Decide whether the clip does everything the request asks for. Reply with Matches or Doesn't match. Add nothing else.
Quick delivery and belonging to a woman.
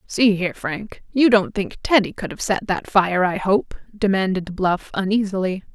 Doesn't match